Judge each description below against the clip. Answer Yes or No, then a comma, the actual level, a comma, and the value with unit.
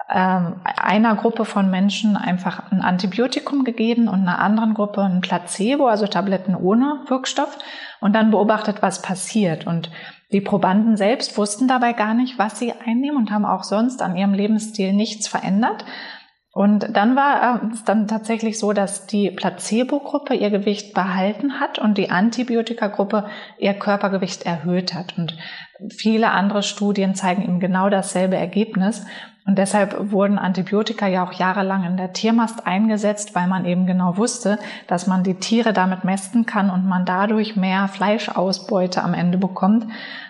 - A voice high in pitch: Yes, high, 205 Hz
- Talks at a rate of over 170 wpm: No, average, 155 wpm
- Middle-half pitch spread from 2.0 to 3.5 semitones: Yes, average, 3.0 semitones